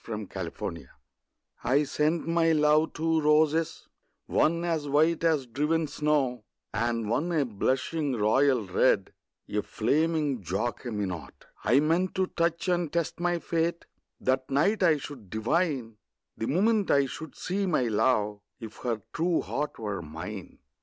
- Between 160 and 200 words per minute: No, average, 145 wpm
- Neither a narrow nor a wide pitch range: No, wide, 6.2 semitones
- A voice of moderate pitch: Yes, medium, 145 Hz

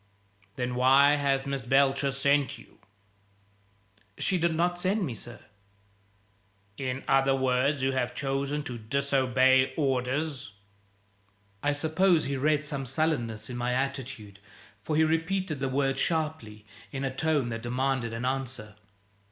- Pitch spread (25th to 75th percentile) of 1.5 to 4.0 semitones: Yes, narrow, 2.6 semitones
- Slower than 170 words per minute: Yes, slow, 135 wpm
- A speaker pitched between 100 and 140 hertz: Yes, low, 135 Hz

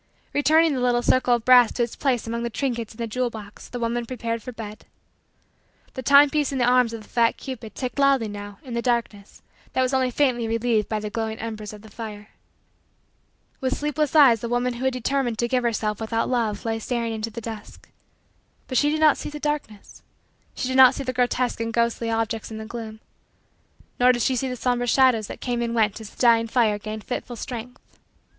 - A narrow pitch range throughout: Yes, narrow, 2.3 semitones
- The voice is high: Yes, high, 235 Hz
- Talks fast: Yes, fast, 220 wpm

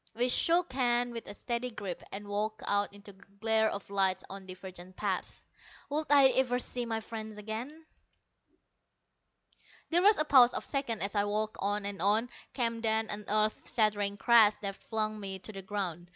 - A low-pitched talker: No, high, 215 Hz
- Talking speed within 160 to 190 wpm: Yes, average, 180 wpm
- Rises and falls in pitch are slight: No, average, 3.0 semitones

